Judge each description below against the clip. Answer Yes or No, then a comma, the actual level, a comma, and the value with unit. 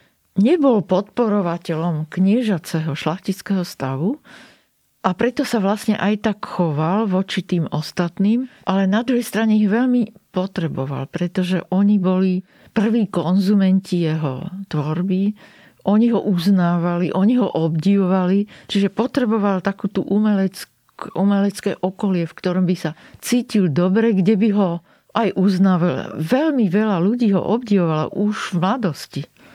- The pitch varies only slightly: No, average, 3.2 semitones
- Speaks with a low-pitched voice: No, high, 195 Hz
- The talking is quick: No, average, 120 wpm